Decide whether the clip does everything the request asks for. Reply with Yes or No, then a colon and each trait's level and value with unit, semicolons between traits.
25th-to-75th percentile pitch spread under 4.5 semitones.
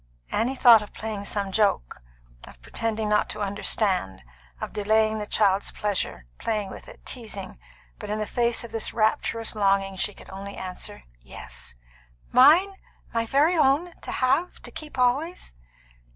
Yes: average, 3.5 semitones